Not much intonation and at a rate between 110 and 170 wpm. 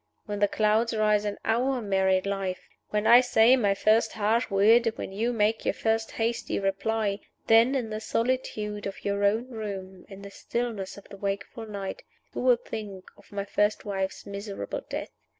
No: narrow, 2.3 semitones; average, 180 wpm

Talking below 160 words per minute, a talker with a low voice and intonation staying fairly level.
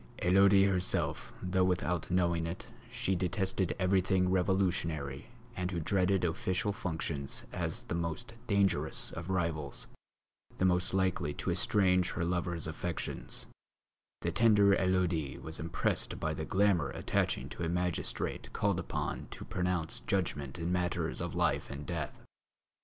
Yes: slow, 135 wpm; very low, 90 Hz; narrow, 2.2 semitones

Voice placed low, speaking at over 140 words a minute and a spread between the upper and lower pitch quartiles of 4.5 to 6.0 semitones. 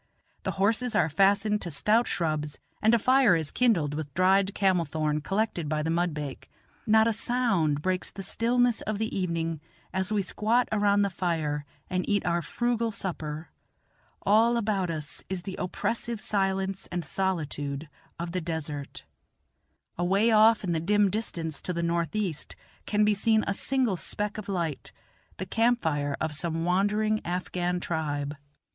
No: medium, 185 Hz; average, 160 wpm; average, 4.8 semitones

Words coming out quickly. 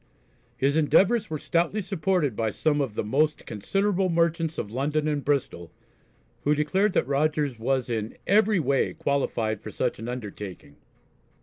No: average, 150 wpm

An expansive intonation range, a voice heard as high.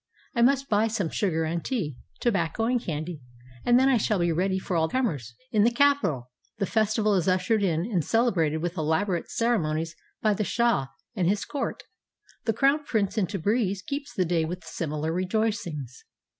Yes: wide, 5.7 semitones; high, 195 Hz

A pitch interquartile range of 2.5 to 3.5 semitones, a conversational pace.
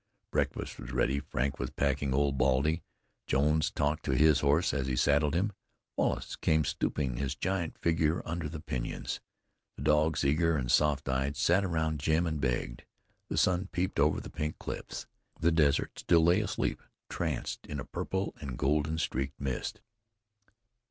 Yes: average, 2.9 semitones; average, 165 wpm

